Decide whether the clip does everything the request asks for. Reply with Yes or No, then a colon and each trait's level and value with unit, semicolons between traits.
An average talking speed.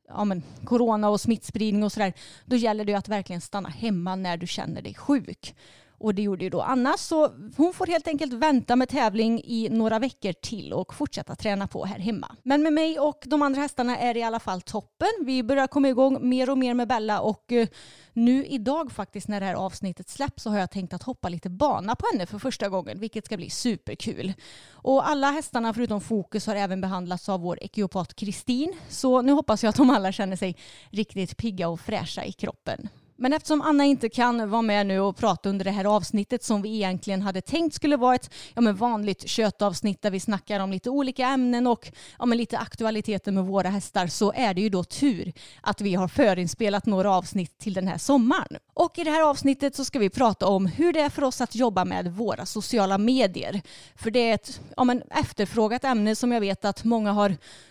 No: fast, 220 wpm